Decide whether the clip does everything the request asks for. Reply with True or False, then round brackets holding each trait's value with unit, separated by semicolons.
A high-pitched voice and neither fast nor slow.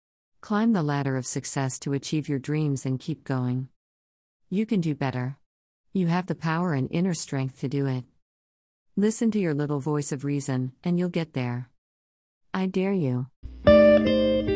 False (135 Hz; 165 wpm)